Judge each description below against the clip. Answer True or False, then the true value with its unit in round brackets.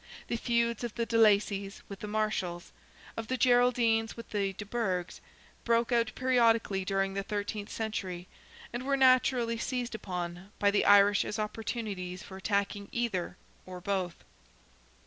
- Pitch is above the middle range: True (210 Hz)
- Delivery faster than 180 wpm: False (150 wpm)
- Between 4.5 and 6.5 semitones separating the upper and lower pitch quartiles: False (3.1 semitones)